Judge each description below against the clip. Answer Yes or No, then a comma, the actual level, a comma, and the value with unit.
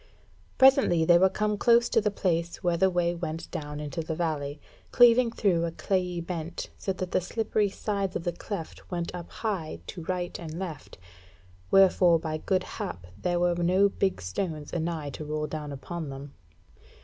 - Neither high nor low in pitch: Yes, medium, 175 Hz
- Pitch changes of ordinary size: Yes, average, 3.3 semitones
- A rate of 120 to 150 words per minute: No, average, 175 wpm